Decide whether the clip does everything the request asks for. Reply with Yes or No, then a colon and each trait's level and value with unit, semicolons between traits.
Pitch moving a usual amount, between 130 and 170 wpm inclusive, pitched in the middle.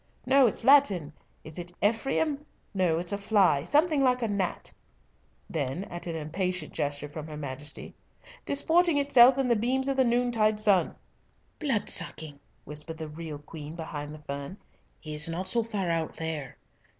No: wide, 7.9 semitones; average, 165 wpm; medium, 180 Hz